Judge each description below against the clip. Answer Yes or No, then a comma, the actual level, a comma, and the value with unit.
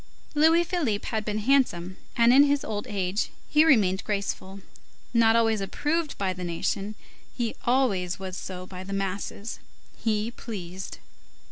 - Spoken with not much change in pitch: No, average, 4.5 semitones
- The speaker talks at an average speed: Yes, average, 145 wpm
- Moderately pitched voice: No, high, 210 Hz